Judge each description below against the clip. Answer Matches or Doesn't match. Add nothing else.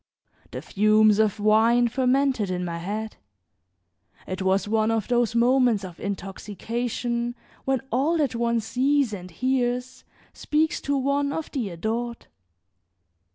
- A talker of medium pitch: Doesn't match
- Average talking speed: Doesn't match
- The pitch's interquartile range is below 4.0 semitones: Matches